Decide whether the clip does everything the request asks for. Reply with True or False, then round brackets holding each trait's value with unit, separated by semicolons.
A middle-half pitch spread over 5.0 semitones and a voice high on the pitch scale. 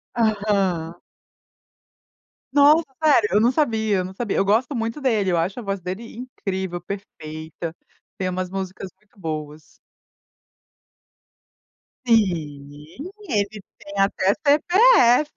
False (4.6 semitones; 200 Hz)